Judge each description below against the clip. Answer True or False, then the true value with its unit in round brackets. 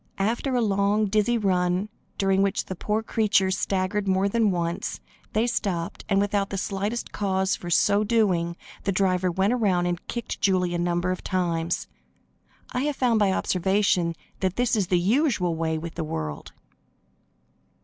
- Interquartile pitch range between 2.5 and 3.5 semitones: True (2.9 semitones)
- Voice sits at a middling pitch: False (195 Hz)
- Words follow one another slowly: False (165 wpm)